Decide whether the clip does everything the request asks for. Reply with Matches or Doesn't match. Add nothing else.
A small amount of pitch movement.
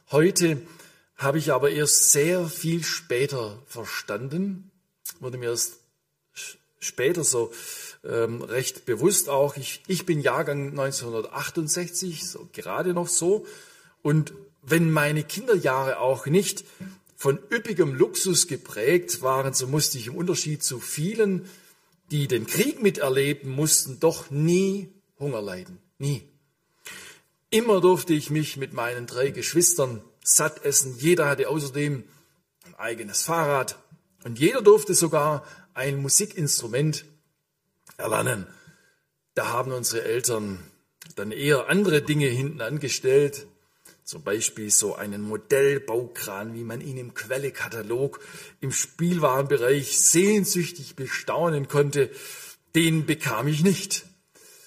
Doesn't match